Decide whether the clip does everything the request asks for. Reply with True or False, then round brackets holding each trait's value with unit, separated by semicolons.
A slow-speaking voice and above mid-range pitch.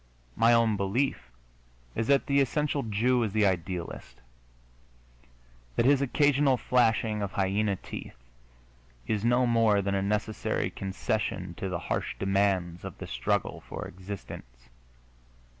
False (130 wpm; 105 Hz)